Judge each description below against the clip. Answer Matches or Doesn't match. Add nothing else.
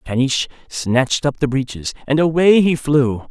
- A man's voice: Matches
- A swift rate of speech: Doesn't match